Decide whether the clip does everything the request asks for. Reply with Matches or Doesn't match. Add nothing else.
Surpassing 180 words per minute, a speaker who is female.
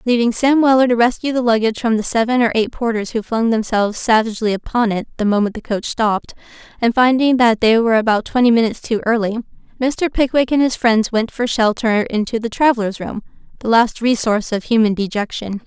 Matches